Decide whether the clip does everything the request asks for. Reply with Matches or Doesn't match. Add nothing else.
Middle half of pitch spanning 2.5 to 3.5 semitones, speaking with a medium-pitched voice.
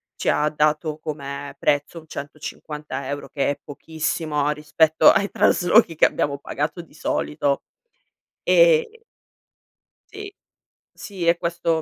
Matches